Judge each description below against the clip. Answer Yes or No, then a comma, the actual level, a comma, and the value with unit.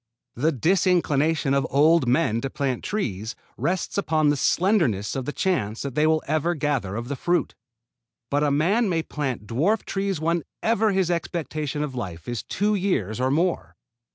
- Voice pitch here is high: No, medium, 150 Hz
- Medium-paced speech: Yes, average, 170 wpm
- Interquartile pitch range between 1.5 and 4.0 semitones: No, average, 5.1 semitones